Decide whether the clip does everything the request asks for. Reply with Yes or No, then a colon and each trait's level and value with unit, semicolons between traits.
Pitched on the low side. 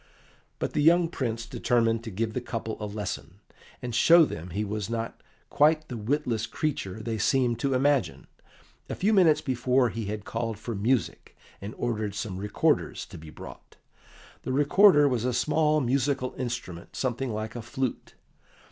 Yes: low, 120 Hz